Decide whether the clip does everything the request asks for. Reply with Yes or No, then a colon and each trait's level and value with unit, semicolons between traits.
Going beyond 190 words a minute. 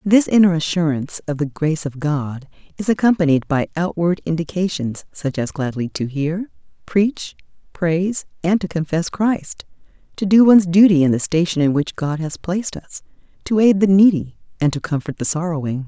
No: average, 175 wpm